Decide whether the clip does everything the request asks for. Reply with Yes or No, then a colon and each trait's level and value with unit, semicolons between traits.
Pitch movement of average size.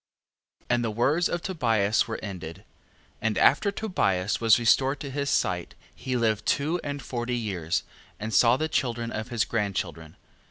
Yes: average, 4.7 semitones